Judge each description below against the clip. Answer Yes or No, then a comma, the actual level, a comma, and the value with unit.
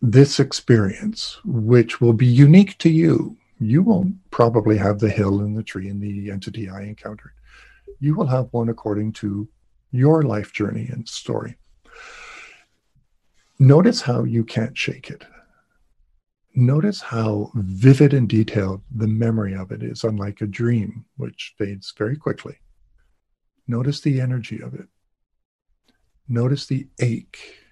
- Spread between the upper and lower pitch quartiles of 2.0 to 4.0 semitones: No, average, 4.6 semitones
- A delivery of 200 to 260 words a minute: No, average, 140 wpm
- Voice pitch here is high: No, low, 115 Hz